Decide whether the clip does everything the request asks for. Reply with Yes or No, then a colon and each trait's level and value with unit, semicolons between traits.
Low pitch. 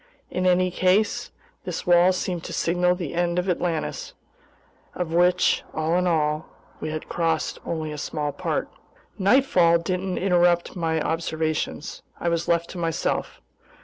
No: medium, 175 Hz